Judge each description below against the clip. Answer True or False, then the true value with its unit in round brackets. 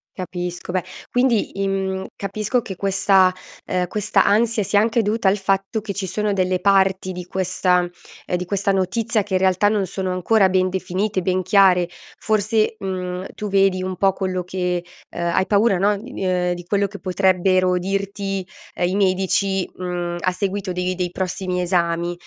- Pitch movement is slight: True (1.7 semitones)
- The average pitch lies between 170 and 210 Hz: True (190 Hz)